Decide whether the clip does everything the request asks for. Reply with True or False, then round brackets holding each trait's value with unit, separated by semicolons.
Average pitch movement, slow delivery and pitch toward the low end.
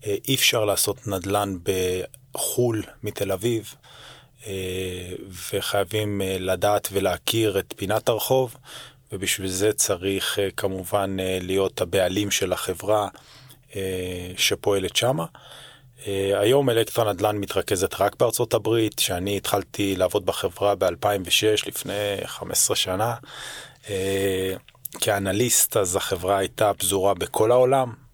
True (3.4 semitones; 95 wpm; 100 Hz)